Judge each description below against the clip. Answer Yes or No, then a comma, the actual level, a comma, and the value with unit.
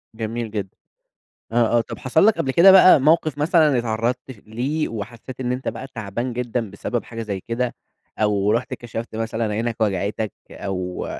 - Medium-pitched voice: No, low, 115 Hz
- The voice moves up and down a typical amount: Yes, average, 3.0 semitones